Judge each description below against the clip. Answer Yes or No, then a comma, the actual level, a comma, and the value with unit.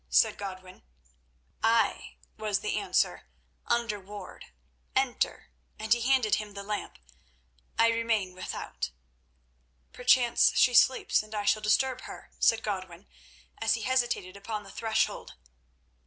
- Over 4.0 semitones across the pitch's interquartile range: No, average, 2.7 semitones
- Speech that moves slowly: Yes, slow, 125 wpm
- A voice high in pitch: Yes, high, 215 Hz